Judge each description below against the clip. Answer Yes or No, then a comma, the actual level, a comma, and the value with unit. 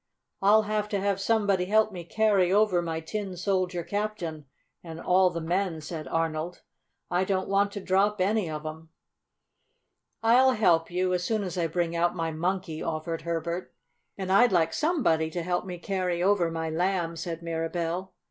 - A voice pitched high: No, medium, 180 Hz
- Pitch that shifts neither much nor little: Yes, average, 3.2 semitones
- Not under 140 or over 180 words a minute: Yes, average, 175 wpm